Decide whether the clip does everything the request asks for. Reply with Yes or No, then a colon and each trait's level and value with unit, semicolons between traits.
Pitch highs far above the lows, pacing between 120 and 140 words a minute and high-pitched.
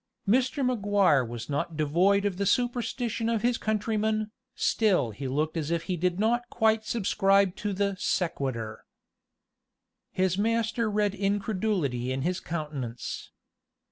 Yes: wide, 5.9 semitones; slow, 135 wpm; high, 200 Hz